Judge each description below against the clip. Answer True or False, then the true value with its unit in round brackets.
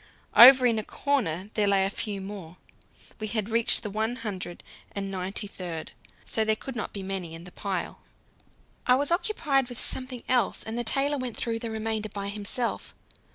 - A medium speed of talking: True (190 wpm)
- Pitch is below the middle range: False (215 Hz)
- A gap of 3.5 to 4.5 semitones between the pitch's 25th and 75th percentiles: True (3.9 semitones)